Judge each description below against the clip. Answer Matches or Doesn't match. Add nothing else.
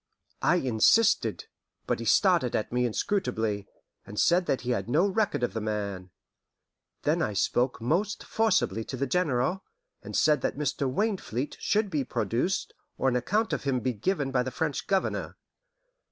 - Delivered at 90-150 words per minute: Doesn't match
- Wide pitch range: Matches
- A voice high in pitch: Doesn't match